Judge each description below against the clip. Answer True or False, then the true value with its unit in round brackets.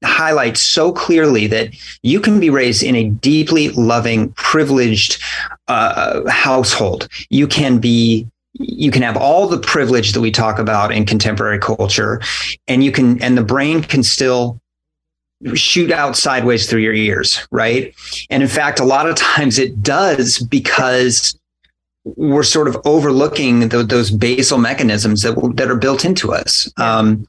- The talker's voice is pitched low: True (125 Hz)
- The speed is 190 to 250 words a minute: False (155 wpm)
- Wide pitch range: False (3.9 semitones)